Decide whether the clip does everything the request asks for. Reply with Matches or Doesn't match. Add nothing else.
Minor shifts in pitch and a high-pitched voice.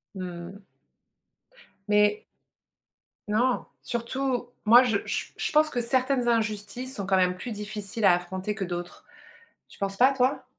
Doesn't match